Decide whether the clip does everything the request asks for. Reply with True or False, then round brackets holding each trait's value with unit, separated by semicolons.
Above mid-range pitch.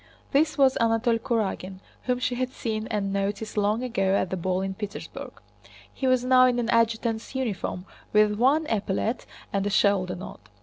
True (220 Hz)